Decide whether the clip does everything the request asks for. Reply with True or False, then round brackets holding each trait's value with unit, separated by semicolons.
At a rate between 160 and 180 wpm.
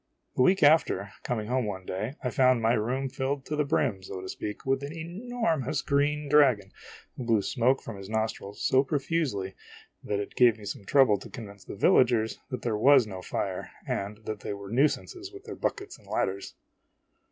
False (195 wpm)